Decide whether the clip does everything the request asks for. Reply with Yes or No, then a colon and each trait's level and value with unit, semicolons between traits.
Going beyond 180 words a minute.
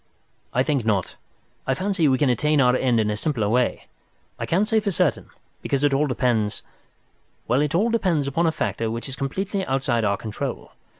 Yes: average, 190 wpm